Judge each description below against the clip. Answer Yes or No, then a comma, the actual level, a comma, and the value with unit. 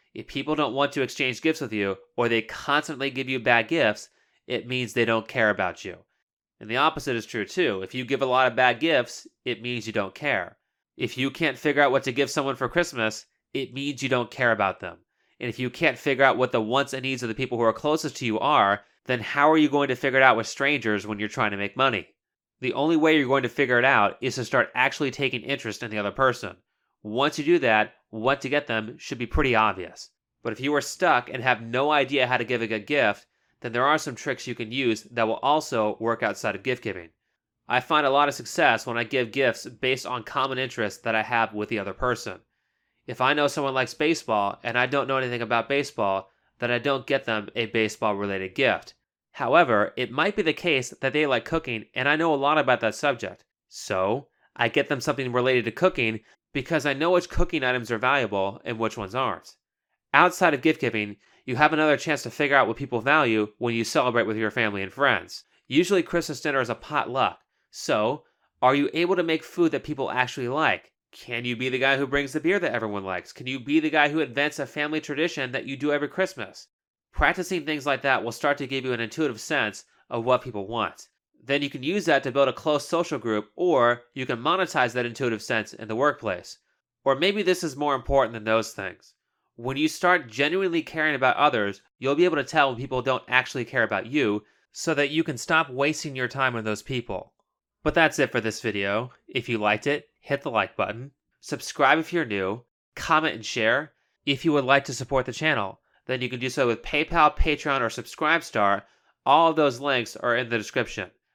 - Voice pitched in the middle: No, low, 130 Hz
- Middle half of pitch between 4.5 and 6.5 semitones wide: No, average, 3.9 semitones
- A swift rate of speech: Yes, fast, 230 wpm